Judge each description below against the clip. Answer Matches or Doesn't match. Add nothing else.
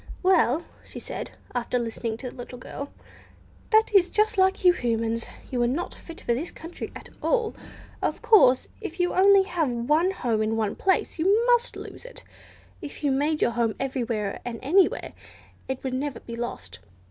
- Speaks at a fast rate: Doesn't match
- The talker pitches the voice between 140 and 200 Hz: Doesn't match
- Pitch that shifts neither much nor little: Doesn't match